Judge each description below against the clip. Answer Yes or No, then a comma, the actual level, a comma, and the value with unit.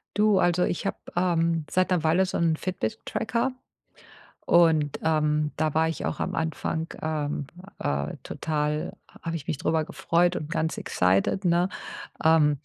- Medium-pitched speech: Yes, medium, 160 Hz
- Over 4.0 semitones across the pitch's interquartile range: No, narrow, 2.5 semitones